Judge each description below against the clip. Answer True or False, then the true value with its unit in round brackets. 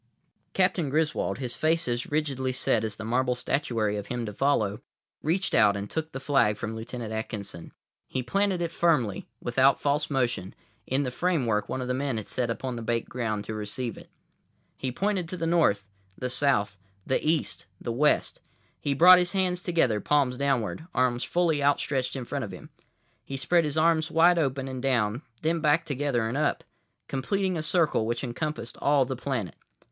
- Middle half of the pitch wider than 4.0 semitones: True (4.9 semitones)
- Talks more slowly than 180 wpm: False (190 wpm)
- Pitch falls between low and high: False (130 Hz)